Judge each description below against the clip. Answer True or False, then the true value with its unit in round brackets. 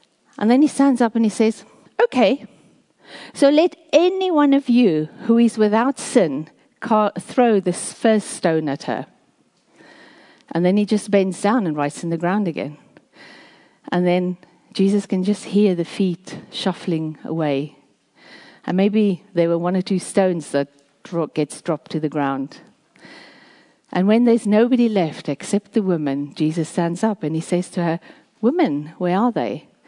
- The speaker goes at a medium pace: True (165 wpm)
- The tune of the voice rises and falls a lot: True (6.1 semitones)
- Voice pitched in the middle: False (200 Hz)